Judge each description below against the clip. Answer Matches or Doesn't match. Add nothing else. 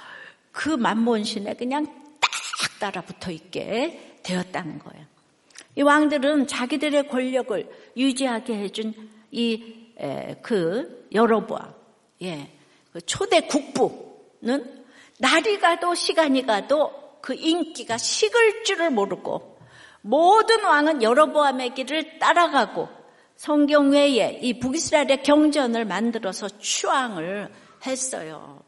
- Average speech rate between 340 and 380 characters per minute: Doesn't match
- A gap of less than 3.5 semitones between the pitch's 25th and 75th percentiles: Doesn't match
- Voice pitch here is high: Matches